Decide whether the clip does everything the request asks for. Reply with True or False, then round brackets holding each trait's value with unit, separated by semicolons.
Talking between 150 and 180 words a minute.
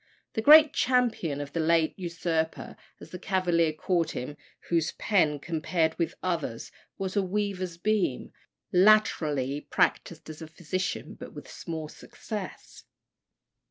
False (135 wpm)